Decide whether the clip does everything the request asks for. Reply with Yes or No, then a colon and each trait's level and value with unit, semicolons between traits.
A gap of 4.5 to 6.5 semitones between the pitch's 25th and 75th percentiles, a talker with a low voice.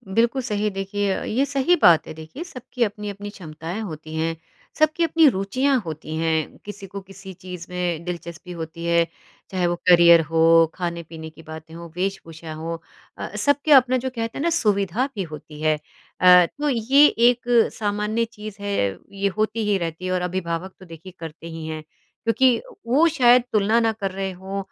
No: wide, 5.4 semitones; high, 190 Hz